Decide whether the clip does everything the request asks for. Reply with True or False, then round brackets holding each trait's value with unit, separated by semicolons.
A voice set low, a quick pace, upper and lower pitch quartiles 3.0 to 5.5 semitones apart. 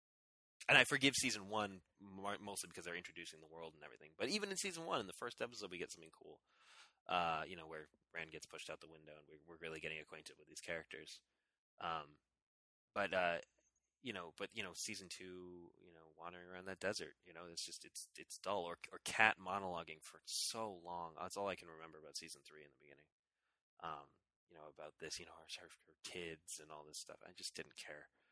True (85 Hz; 220 wpm; 3.8 semitones)